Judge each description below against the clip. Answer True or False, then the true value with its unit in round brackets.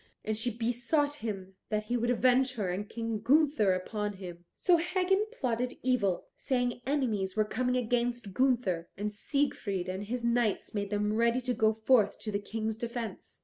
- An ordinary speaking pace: True (175 wpm)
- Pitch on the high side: True (230 Hz)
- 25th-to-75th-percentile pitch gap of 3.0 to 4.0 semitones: True (3.4 semitones)